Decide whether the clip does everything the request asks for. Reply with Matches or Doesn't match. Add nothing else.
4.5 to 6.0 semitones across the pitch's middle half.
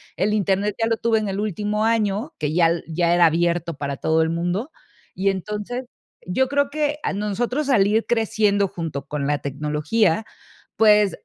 Matches